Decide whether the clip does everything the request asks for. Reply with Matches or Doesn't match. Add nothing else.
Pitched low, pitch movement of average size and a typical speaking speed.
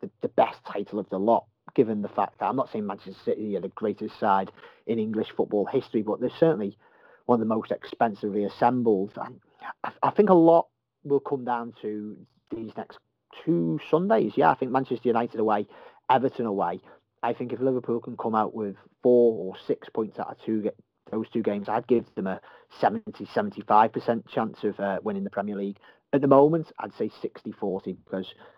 Matches